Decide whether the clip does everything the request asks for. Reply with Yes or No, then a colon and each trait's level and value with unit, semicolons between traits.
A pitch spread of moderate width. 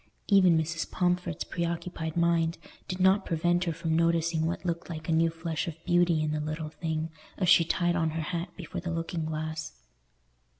No: narrow, 1.6 semitones